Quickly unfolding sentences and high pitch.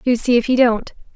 Yes: fast, 260 wpm; high, 235 Hz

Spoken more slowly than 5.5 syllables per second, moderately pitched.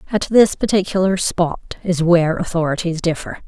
Yes: 5.2 syllables/s; medium, 175 Hz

